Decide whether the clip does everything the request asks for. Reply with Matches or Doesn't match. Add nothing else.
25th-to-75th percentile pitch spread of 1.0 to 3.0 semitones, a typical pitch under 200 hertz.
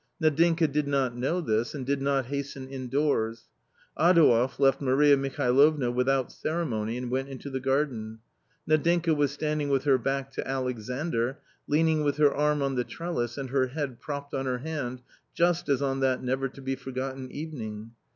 Matches